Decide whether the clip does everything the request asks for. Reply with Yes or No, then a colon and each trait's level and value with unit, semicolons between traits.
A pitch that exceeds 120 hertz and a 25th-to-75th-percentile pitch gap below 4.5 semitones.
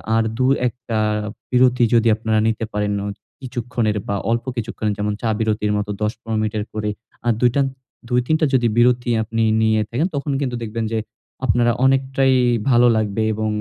No: low, 115 Hz; narrow, 2.5 semitones